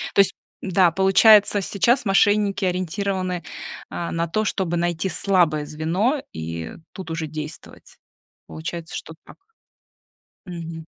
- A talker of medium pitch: Yes, medium, 180 Hz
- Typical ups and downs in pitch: Yes, average, 3.4 semitones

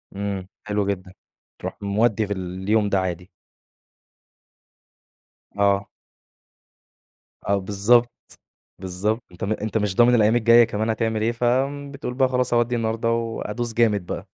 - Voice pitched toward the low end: Yes, low, 110 Hz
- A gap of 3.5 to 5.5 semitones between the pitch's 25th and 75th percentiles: No, average, 2.8 semitones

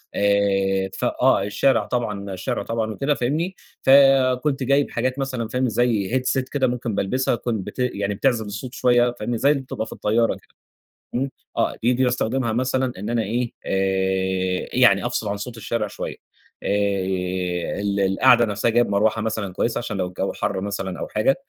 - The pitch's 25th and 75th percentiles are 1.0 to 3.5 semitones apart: No, average, 4.0 semitones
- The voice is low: Yes, low, 115 Hz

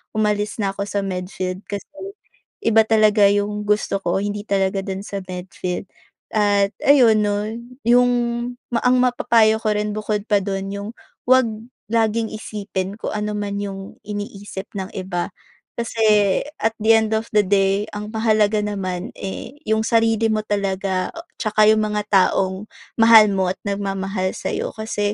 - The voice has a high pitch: Yes, high, 205 Hz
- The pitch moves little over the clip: Yes, narrow, 1.9 semitones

